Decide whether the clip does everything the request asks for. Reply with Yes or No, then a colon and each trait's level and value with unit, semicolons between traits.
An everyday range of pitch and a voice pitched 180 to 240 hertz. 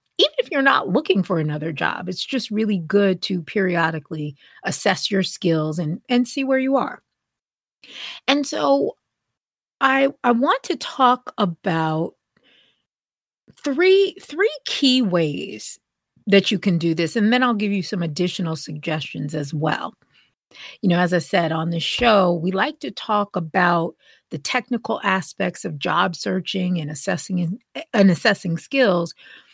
No: wide, 6.7 semitones; high, 190 Hz